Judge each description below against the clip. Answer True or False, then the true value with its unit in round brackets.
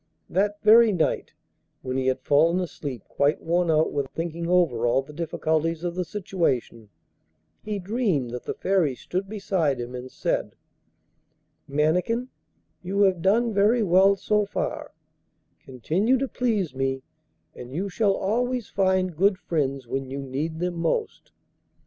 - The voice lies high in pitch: False (175 Hz)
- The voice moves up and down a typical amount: False (6.1 semitones)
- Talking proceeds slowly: False (150 wpm)